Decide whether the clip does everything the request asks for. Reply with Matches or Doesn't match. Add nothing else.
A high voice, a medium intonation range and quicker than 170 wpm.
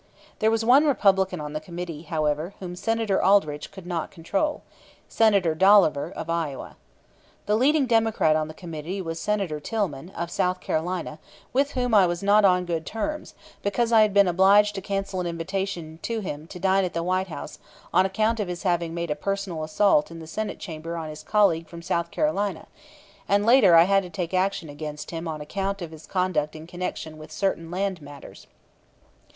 Doesn't match